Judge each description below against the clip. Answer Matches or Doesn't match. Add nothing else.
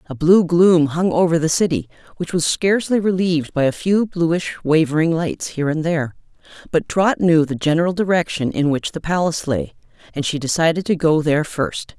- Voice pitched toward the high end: Doesn't match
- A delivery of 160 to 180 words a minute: Doesn't match